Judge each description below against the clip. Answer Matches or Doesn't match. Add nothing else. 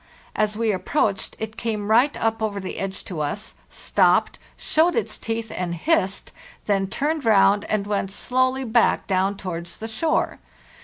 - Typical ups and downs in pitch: Matches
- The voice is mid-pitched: Doesn't match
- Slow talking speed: Doesn't match